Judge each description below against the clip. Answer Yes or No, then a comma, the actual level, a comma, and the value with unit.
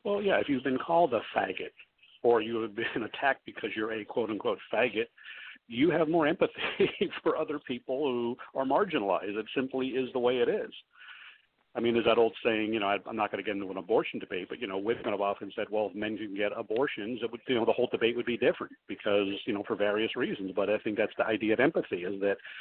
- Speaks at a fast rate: Yes, fast, 240 wpm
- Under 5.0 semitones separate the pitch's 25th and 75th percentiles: No, wide, 5.4 semitones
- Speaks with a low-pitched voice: Yes, low, 120 Hz